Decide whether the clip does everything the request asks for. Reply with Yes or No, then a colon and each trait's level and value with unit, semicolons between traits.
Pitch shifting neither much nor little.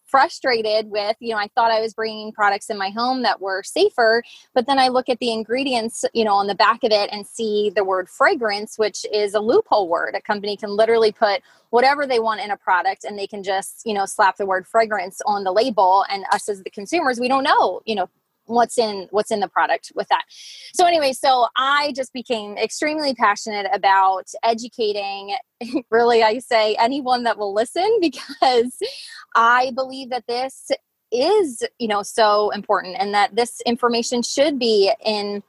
Yes: average, 3.8 semitones